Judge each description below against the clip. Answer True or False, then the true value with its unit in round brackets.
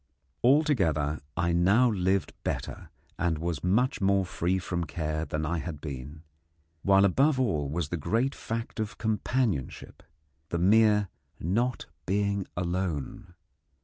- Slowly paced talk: True (130 wpm)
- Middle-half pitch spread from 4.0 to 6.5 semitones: True (5.0 semitones)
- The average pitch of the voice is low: True (90 Hz)